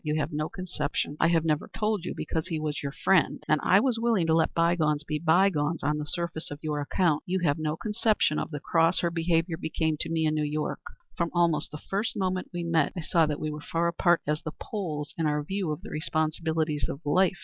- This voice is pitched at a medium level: Yes, medium, 160 Hz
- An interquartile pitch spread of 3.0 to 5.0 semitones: No, narrow, 2.4 semitones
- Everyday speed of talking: No, fast, 235 wpm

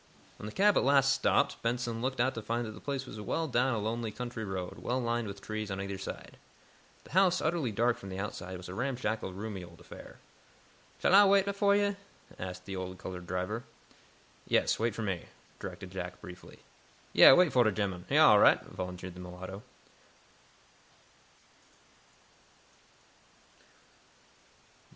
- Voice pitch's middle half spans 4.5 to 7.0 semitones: Yes, wide, 5.6 semitones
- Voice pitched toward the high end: No, low, 110 Hz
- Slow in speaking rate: No, average, 165 wpm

